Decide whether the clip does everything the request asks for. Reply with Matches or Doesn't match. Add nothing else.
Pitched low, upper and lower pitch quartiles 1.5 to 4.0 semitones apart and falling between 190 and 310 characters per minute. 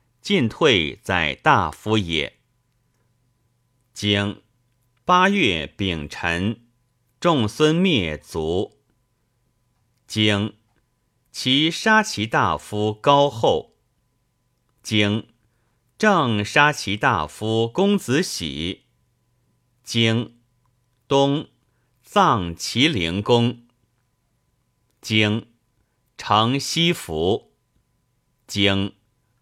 Doesn't match